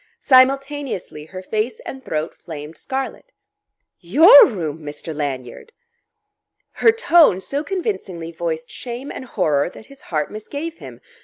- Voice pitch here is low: No, high, 215 Hz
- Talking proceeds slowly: Yes, slow, 130 wpm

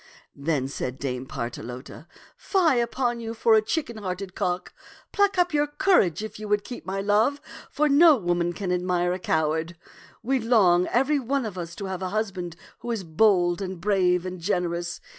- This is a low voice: No, high, 190 Hz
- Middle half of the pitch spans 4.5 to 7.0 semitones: Yes, average, 5.1 semitones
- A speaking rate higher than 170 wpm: Yes, average, 195 wpm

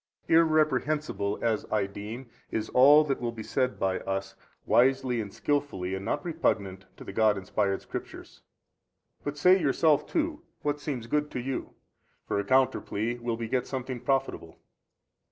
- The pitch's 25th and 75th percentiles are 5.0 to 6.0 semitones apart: Yes, wide, 5.6 semitones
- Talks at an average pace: Yes, average, 160 wpm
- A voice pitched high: No, low, 125 Hz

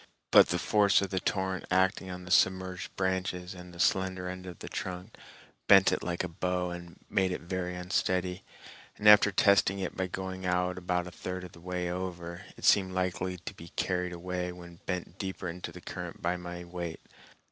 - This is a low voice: Yes, very low, 90 Hz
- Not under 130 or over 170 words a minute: No, average, 200 wpm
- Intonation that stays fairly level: Yes, narrow, 0.9 semitones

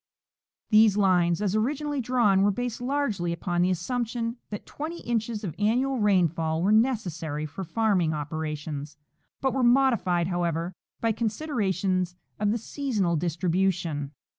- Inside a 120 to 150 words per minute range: Yes, average, 140 wpm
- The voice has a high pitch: Yes, high, 200 Hz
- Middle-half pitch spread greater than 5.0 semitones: Yes, wide, 5.4 semitones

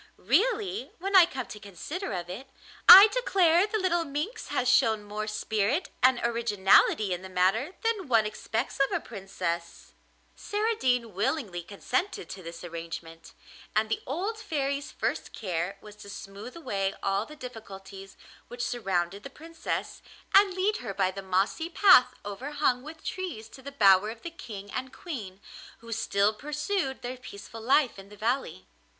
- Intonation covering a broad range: Yes, wide, 8.0 semitones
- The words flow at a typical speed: Yes, average, 160 wpm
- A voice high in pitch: Yes, high, 235 Hz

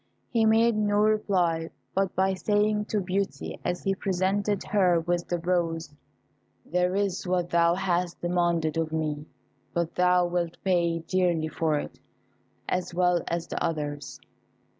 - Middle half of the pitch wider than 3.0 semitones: No, narrow, 2.4 semitones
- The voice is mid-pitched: Yes, medium, 180 Hz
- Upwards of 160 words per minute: No, average, 145 wpm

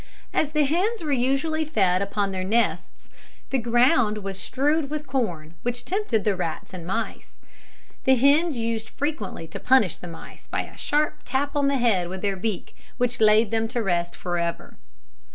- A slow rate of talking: No, average, 180 wpm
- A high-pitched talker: Yes, high, 230 Hz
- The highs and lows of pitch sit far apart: Yes, wide, 6.5 semitones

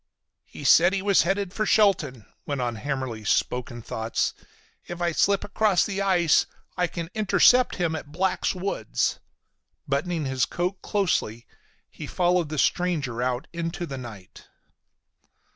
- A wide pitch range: Yes, wide, 6.4 semitones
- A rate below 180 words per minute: Yes, average, 145 wpm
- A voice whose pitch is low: No, medium, 170 Hz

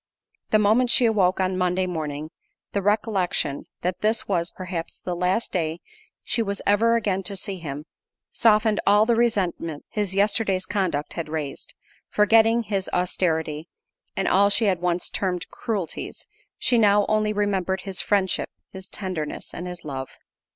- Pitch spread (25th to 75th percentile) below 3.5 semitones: Yes, average, 3.1 semitones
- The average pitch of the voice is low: No, high, 190 Hz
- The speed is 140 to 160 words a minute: Yes, average, 155 wpm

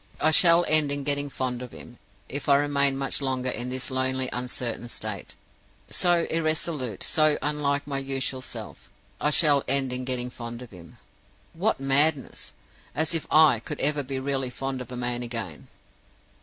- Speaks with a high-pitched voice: No, low, 135 Hz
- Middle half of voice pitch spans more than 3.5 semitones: No, average, 2.7 semitones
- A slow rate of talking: No, average, 170 wpm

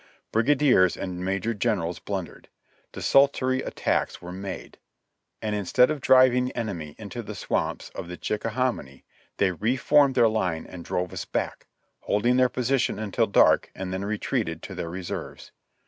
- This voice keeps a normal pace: Yes, average, 155 wpm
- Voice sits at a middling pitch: No, low, 105 Hz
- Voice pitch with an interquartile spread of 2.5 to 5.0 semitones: No, wide, 5.5 semitones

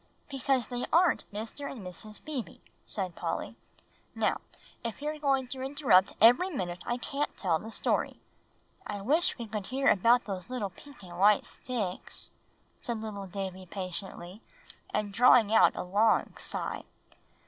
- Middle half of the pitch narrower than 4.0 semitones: No, average, 5.2 semitones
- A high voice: Yes, high, 220 Hz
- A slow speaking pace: No, average, 150 wpm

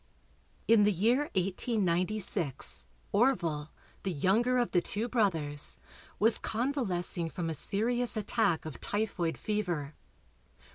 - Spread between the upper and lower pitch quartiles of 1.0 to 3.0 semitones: No, average, 5.2 semitones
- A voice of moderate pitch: No, high, 195 Hz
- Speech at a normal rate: No, slow, 110 wpm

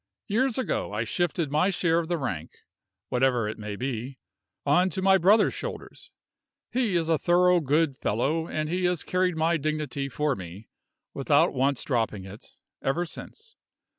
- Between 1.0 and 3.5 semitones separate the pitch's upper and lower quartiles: No, wide, 5.6 semitones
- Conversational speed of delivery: Yes, average, 165 wpm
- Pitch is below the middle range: No, medium, 155 Hz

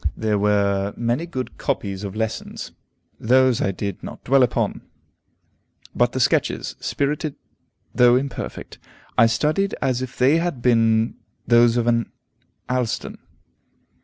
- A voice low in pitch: Yes, low, 120 Hz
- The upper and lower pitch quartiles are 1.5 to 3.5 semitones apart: Yes, average, 2.9 semitones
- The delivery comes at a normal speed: No, slow, 130 wpm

